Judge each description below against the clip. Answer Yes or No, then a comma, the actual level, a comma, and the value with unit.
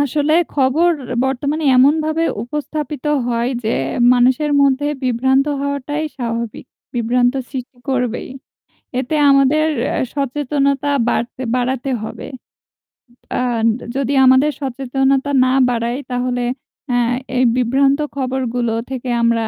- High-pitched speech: Yes, very high, 260 Hz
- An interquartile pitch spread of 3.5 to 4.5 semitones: No, narrow, 2.4 semitones